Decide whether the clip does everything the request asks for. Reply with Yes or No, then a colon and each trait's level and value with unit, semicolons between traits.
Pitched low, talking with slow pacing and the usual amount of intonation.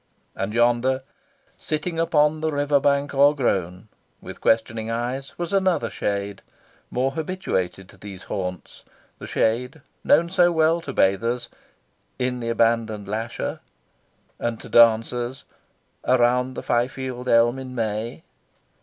Yes: low, 120 Hz; slow, 125 wpm; average, 4.1 semitones